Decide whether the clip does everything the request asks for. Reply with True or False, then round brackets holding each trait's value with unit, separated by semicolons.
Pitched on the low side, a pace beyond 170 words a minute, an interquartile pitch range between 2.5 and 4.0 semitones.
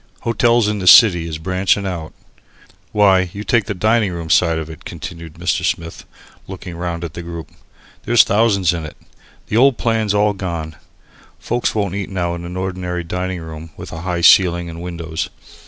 True (90 Hz; 185 wpm; 3.4 semitones)